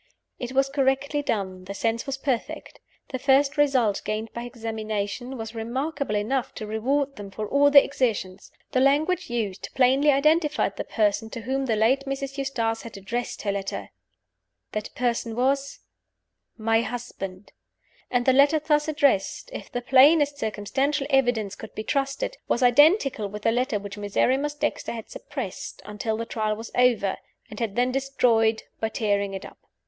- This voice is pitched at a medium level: No, high, 245 Hz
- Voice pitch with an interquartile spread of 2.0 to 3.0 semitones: No, average, 4.1 semitones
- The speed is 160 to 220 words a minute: Yes, average, 165 wpm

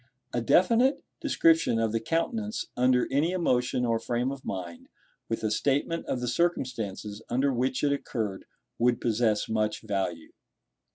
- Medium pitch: No, low, 125 Hz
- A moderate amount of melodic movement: Yes, average, 4.3 semitones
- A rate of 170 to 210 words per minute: No, average, 150 wpm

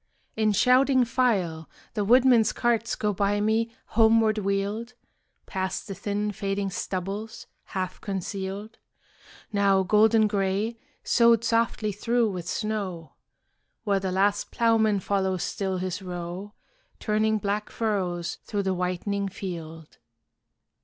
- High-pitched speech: Yes, high, 205 Hz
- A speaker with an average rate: No, slow, 120 wpm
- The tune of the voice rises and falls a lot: No, narrow, 2.6 semitones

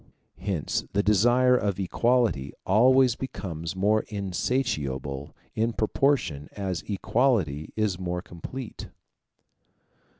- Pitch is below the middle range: Yes, low, 100 Hz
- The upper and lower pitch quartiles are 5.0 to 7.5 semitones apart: Yes, wide, 5.6 semitones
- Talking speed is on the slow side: Yes, slow, 95 wpm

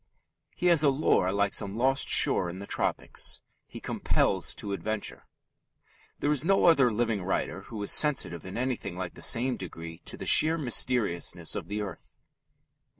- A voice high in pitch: No, low, 110 Hz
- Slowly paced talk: No, average, 170 wpm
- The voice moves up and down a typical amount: No, wide, 6.0 semitones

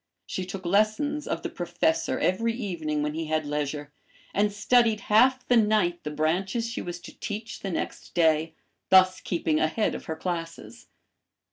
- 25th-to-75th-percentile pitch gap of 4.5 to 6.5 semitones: Yes, average, 5.1 semitones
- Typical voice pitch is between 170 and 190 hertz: Yes, medium, 185 Hz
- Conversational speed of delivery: Yes, average, 165 wpm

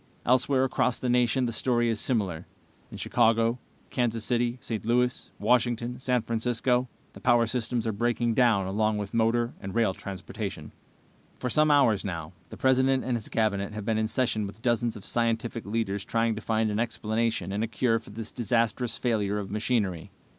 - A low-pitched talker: Yes, low, 115 Hz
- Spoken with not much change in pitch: Yes, narrow, 2.3 semitones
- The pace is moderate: Yes, average, 180 wpm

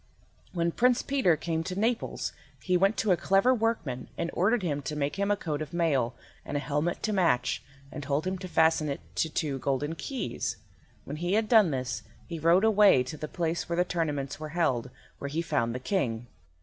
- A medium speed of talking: No, fast, 210 wpm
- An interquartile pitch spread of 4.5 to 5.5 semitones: Yes, average, 5.1 semitones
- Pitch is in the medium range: Yes, medium, 165 Hz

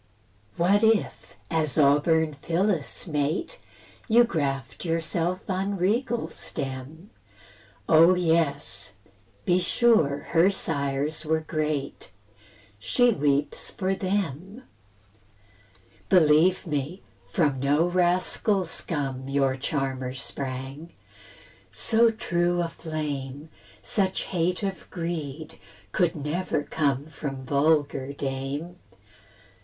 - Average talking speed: No, slow, 95 wpm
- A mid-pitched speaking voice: Yes, medium, 160 Hz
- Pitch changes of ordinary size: Yes, average, 4.4 semitones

